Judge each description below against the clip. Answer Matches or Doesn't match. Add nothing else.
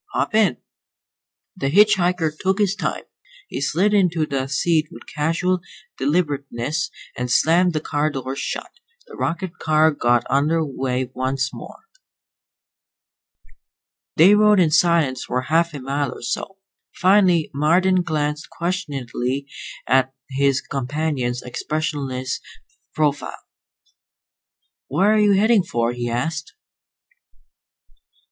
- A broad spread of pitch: Doesn't match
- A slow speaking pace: Matches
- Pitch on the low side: Doesn't match